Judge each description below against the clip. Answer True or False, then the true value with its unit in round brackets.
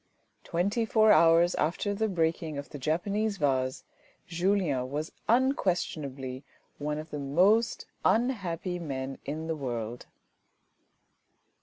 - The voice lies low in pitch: False (165 Hz)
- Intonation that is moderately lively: False (5.9 semitones)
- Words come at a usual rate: False (115 wpm)